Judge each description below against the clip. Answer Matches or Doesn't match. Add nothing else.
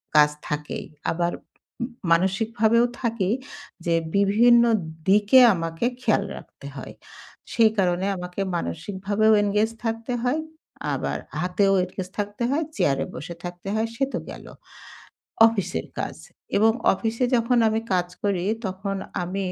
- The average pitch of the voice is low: Doesn't match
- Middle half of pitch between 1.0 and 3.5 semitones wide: Doesn't match